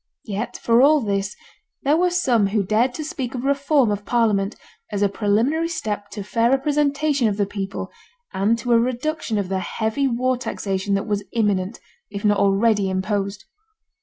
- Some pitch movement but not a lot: Yes, average, 4.3 semitones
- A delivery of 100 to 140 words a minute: No, average, 175 wpm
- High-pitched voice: Yes, high, 220 Hz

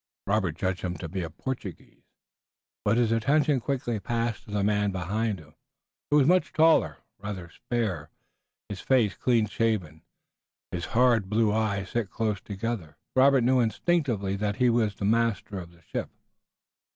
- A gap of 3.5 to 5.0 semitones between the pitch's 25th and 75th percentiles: Yes, average, 3.8 semitones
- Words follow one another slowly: No, average, 155 wpm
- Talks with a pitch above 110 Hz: No, low, 105 Hz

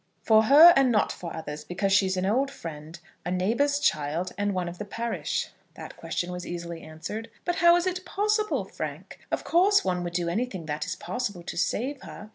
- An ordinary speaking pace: No, fast, 215 wpm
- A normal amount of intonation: No, wide, 7.8 semitones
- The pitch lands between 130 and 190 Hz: No, high, 200 Hz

